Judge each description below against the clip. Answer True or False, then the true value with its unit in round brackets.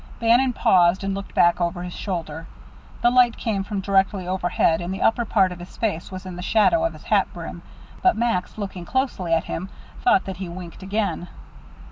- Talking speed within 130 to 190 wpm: False (200 wpm)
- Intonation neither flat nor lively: True (3.7 semitones)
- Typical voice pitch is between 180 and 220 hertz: True (190 Hz)